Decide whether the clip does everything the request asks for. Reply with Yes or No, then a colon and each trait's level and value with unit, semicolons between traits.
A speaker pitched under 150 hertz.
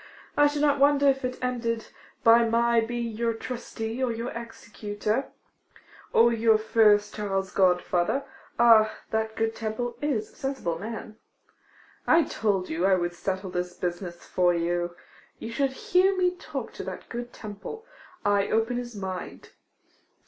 No: high, 225 Hz